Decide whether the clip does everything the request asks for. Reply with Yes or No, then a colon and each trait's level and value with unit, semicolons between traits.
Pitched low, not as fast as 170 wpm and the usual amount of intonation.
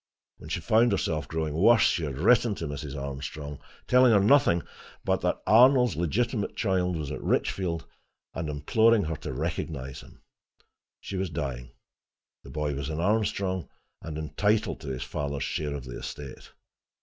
No: very low, 80 Hz; average, 160 wpm; wide, 6.0 semitones